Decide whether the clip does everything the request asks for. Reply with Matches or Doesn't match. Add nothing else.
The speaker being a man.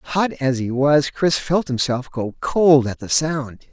Matches